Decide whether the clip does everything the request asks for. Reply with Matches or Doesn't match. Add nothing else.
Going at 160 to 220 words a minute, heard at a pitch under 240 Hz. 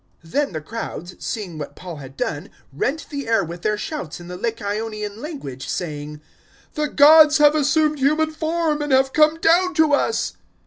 Doesn't match